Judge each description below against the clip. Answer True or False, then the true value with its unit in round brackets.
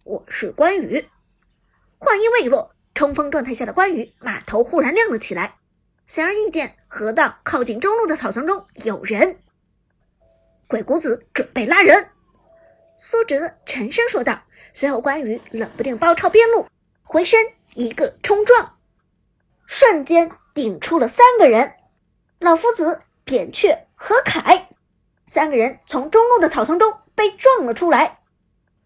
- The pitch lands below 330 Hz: False (335 Hz)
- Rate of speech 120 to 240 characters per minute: True (210 characters per minute)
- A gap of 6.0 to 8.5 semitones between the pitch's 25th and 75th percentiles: True (7.5 semitones)